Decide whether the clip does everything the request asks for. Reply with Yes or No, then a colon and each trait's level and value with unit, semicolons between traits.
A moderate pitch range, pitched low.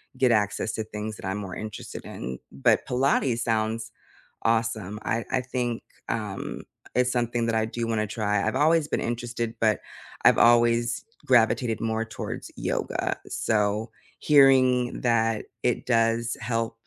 No: narrow, 1.8 semitones; low, 115 Hz